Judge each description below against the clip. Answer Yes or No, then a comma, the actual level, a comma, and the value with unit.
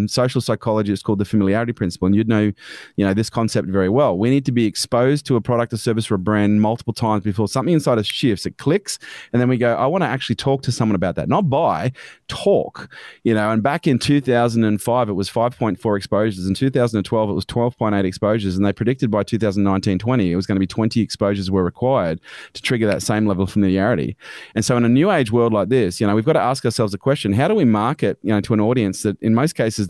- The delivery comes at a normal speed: No, fast, 245 wpm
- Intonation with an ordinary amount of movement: Yes, average, 3.1 semitones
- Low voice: Yes, low, 110 Hz